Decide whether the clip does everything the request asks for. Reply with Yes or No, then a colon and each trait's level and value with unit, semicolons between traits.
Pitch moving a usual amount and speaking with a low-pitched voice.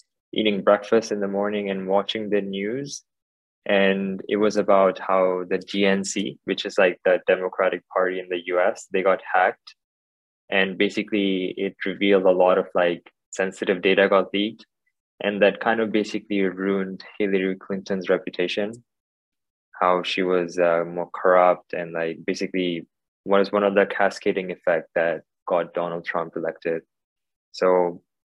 No: narrow, 2.0 semitones; very low, 95 Hz